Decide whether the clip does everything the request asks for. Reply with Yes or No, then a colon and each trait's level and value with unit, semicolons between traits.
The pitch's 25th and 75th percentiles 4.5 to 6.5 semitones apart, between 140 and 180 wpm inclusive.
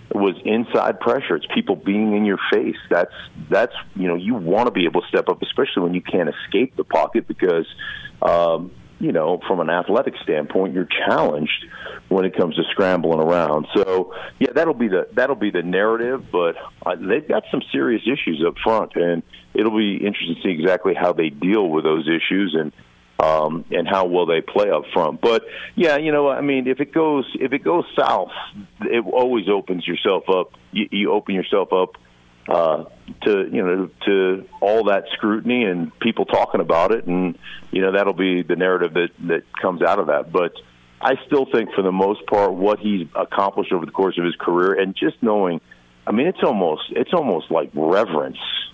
No: average, 5.3 semitones; average, 200 wpm